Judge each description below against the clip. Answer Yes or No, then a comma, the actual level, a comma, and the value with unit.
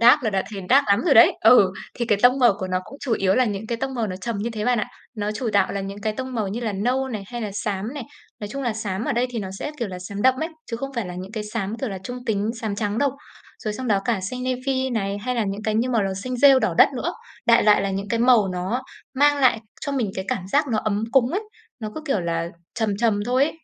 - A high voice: Yes, high, 220 Hz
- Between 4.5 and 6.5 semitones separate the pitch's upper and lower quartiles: No, average, 3.9 semitones